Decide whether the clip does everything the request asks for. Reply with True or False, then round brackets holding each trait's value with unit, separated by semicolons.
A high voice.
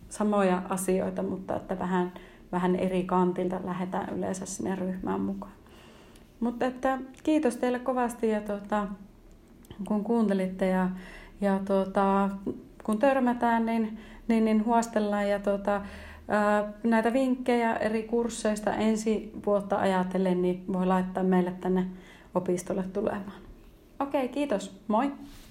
True (205 Hz)